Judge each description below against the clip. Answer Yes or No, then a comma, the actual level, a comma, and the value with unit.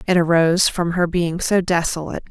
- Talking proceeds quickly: No, average, 180 wpm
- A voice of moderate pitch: Yes, medium, 170 Hz